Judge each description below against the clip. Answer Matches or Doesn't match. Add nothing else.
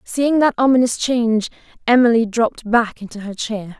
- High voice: Matches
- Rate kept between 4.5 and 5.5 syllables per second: Matches